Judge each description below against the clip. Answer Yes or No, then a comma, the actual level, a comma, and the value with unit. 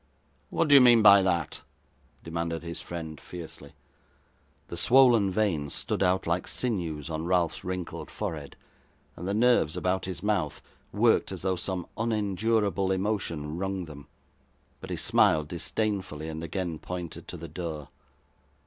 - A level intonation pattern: No, average, 3.6 semitones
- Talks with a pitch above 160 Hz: No, very low, 90 Hz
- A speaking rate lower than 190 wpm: Yes, average, 145 wpm